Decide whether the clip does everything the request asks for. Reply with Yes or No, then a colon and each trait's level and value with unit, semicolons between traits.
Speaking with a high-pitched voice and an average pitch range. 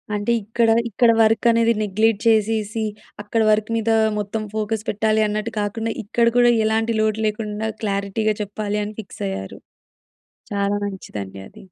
No: high, 215 Hz; narrow, 1.5 semitones